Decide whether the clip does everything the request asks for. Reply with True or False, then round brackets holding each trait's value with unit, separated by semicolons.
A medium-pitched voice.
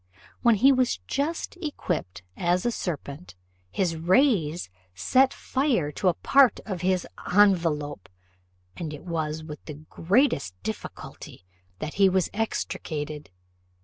True (180 Hz)